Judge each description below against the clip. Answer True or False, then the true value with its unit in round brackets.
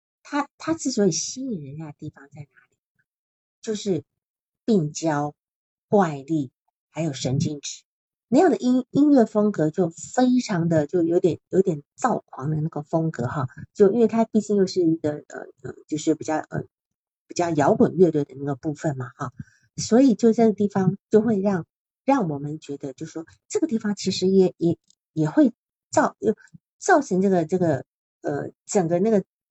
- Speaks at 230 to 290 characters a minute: True (245 characters per minute)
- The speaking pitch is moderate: True (170 Hz)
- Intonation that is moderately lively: False (5.9 semitones)